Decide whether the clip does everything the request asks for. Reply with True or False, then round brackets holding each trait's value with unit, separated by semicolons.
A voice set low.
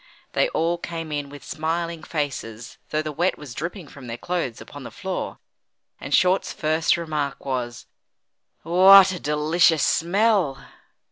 False (160 Hz)